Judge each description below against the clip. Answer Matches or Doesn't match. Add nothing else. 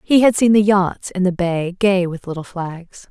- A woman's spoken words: Matches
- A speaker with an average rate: Doesn't match